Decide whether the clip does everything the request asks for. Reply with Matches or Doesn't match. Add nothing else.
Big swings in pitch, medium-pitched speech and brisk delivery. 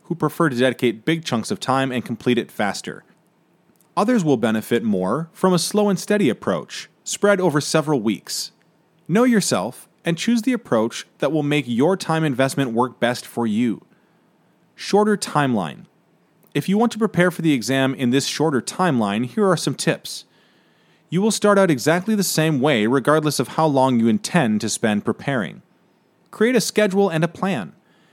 Doesn't match